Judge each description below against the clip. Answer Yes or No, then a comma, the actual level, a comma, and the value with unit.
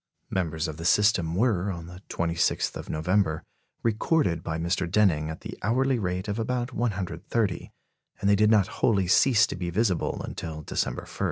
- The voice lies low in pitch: Yes, very low, 95 Hz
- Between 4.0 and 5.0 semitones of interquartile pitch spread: Yes, average, 4.4 semitones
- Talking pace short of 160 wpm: No, average, 175 wpm